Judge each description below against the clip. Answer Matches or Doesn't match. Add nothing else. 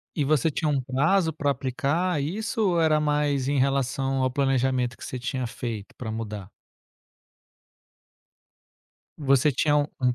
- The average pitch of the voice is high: Doesn't match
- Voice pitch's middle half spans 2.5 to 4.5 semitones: Matches